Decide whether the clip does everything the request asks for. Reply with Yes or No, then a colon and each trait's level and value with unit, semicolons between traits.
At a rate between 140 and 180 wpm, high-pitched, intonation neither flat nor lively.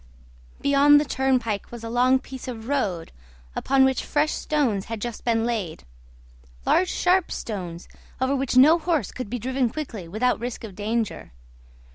Yes: average, 160 wpm; very high, 250 Hz; average, 3.7 semitones